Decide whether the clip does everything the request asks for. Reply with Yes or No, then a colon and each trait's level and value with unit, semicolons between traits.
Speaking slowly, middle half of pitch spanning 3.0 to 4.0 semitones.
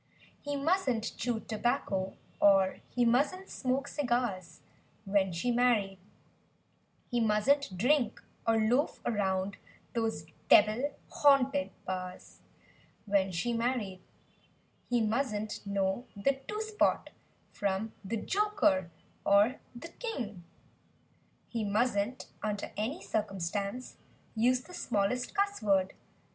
No: slow, 105 wpm; average, 4.4 semitones